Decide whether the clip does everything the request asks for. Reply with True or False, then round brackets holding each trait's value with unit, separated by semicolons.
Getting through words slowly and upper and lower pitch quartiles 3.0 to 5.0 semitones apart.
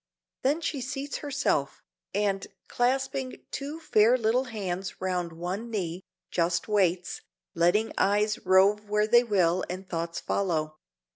False (130 wpm; 5.4 semitones)